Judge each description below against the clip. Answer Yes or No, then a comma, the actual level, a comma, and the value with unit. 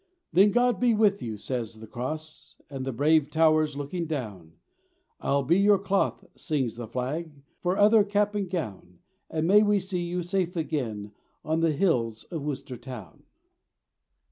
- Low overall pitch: No, medium, 155 Hz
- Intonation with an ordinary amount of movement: No, wide, 7.0 semitones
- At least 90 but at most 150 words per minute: No, average, 170 wpm